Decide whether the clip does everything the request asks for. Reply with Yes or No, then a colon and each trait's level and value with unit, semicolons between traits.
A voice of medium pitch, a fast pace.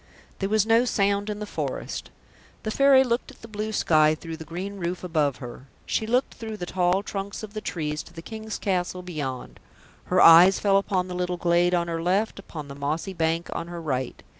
Yes: medium, 180 Hz; fast, 215 wpm